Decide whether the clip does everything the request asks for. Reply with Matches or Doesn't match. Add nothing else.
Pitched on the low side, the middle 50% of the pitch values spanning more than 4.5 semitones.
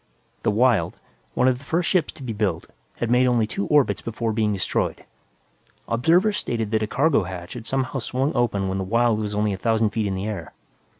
Doesn't match